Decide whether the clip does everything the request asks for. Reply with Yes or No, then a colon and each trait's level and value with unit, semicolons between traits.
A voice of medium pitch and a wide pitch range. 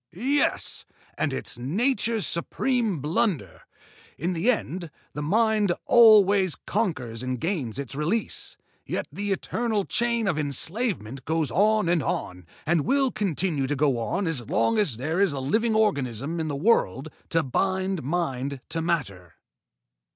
Yes: medium, 170 Hz; wide, 7.3 semitones